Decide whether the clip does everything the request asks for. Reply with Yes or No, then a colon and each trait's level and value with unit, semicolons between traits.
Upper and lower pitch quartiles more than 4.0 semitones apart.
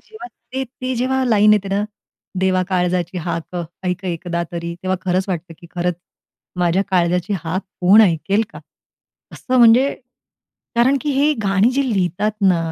Yes: average, 4.8 semitones